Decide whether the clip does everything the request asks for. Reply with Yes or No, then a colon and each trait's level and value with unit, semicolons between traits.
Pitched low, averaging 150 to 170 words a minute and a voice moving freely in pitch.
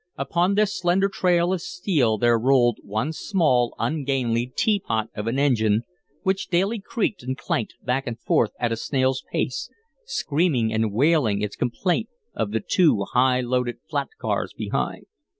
Yes: low, 130 Hz; average, 155 wpm; wide, 7.1 semitones